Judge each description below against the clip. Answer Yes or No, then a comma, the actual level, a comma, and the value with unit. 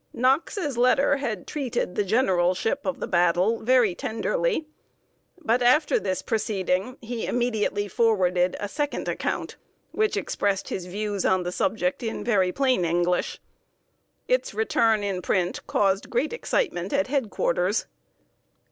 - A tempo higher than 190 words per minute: No, slow, 135 wpm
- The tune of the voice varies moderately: No, wide, 6.5 semitones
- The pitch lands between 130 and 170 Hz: No, high, 225 Hz